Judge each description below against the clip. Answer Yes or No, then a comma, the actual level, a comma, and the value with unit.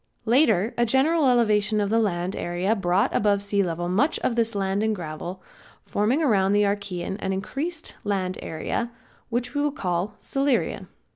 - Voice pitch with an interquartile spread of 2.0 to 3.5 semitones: No, average, 4.0 semitones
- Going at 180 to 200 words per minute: No, average, 160 wpm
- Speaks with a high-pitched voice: Yes, high, 205 Hz